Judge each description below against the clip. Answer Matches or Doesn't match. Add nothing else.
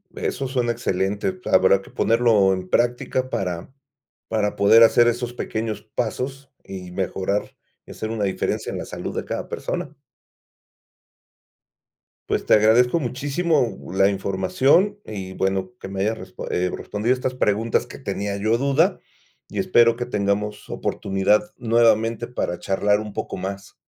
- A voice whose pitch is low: Matches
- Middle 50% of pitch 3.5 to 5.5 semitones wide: Matches